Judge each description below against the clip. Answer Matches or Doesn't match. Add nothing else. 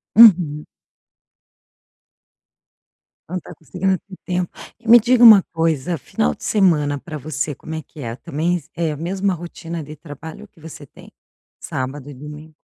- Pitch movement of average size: Matches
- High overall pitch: Doesn't match